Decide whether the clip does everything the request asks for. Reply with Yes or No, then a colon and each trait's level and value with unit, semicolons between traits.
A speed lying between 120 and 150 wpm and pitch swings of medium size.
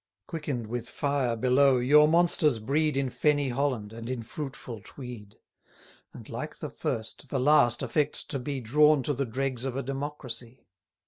No: average, 170 wpm; average, 3.2 semitones